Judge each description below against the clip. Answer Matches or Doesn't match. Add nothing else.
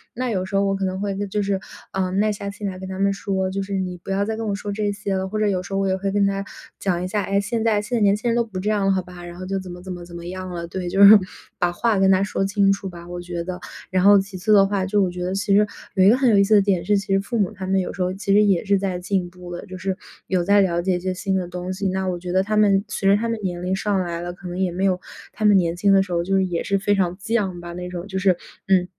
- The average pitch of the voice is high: Matches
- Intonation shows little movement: Matches